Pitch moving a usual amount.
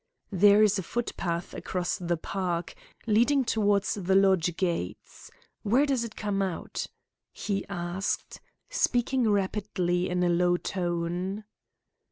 Yes: average, 3.1 semitones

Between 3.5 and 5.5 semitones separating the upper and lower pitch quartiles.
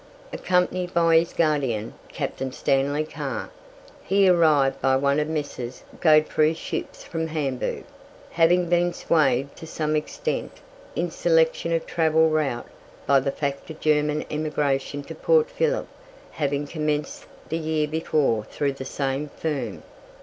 No: average, 2.8 semitones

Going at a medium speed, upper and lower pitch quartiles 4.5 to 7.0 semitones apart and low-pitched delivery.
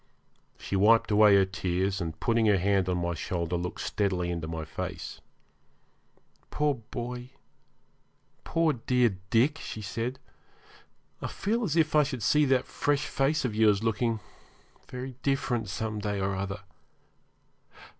Yes: average, 145 wpm; average, 5.1 semitones; low, 110 Hz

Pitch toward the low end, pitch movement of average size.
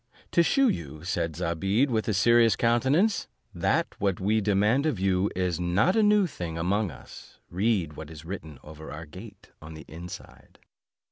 No: very low, 95 Hz; wide, 5.9 semitones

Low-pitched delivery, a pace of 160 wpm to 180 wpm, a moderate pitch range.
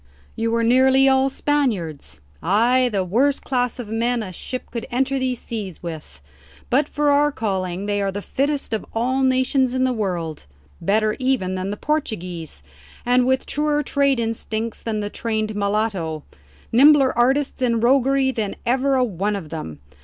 No: high, 235 Hz; average, 170 wpm; average, 4.6 semitones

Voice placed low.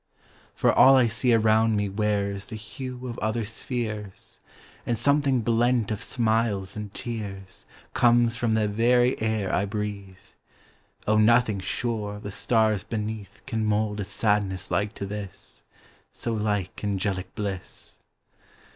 Yes: low, 110 Hz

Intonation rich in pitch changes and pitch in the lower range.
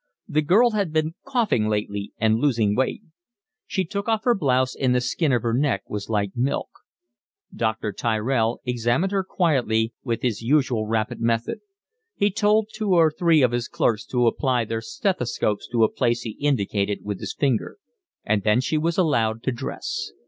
Yes: wide, 6.0 semitones; low, 125 Hz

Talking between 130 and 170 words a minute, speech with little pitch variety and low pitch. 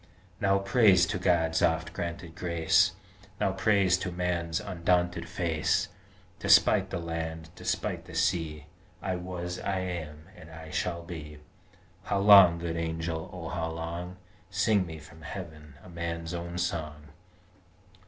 Yes: average, 140 wpm; narrow, 2.0 semitones; very low, 85 Hz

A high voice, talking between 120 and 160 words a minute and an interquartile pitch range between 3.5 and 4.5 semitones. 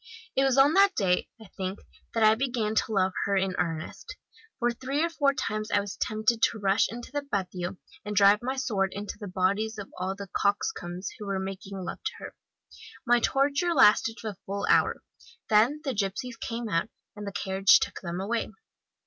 No: high, 210 Hz; average, 195 wpm; average, 3.8 semitones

